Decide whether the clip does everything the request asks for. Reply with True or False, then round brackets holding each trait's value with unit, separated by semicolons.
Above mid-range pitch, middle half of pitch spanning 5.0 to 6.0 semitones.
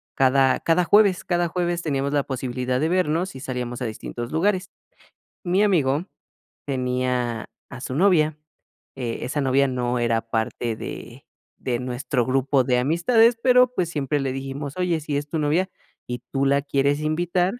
False (140 Hz; 5.3 semitones)